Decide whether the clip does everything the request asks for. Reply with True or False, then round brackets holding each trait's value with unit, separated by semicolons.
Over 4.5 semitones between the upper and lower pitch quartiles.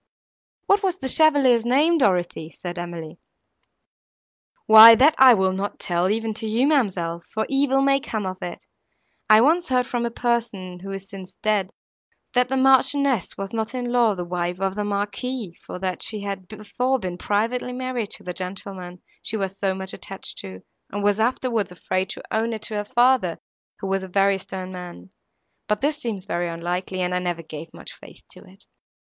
True (5.1 semitones)